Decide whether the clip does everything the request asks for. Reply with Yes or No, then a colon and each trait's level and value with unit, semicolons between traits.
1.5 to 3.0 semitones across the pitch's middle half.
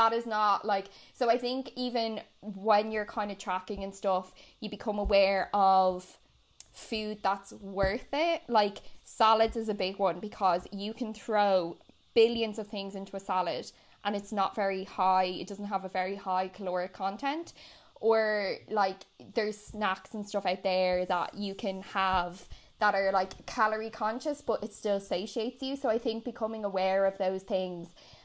Yes: narrow, 2.5 semitones